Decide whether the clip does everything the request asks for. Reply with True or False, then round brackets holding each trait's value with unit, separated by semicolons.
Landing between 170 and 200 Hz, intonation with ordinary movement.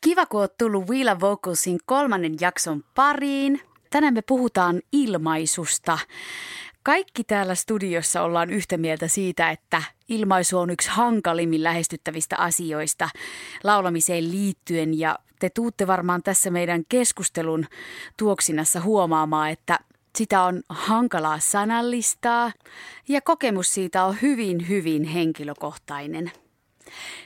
False (185 Hz; 5.9 semitones)